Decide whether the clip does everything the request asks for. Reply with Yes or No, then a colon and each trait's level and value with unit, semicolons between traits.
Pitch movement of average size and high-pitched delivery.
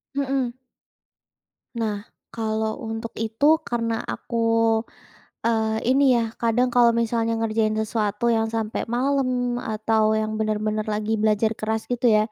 No: narrow, 1.6 semitones; high, 225 Hz